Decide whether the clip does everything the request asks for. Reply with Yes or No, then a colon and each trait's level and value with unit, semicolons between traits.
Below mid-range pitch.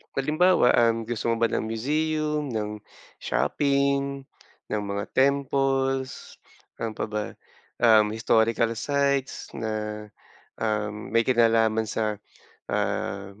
Yes: low, 115 Hz